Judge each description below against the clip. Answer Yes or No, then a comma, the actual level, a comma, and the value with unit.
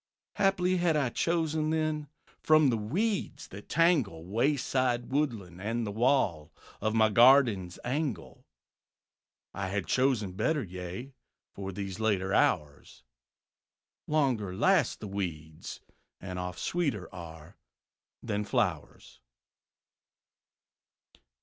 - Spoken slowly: Yes, slow, 105 wpm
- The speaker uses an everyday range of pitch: No, wide, 7.9 semitones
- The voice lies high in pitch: No, low, 110 Hz